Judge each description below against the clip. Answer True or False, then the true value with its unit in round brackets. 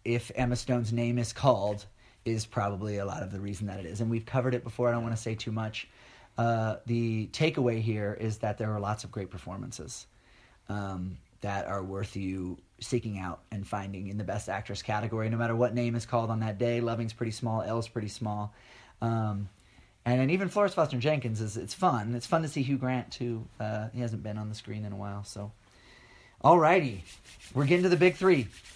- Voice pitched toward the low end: True (115 Hz)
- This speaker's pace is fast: True (215 wpm)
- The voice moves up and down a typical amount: True (3.0 semitones)